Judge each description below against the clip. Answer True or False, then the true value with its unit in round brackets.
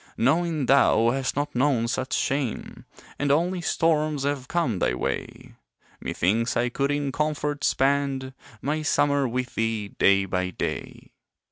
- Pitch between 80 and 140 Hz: True (135 Hz)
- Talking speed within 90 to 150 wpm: True (140 wpm)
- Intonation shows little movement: False (3.6 semitones)